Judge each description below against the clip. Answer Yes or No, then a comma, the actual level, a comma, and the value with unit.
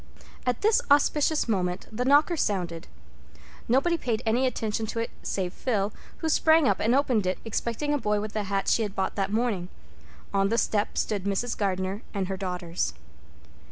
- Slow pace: No, average, 180 wpm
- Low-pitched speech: No, high, 215 Hz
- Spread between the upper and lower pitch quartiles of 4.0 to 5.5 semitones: Yes, average, 4.5 semitones